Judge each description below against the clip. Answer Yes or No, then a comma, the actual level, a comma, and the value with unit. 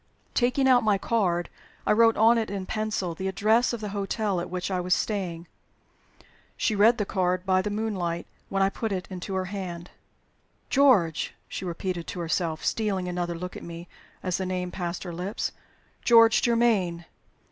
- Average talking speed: Yes, average, 180 wpm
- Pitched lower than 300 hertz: Yes, high, 190 Hz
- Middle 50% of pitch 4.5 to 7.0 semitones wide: No, average, 3.4 semitones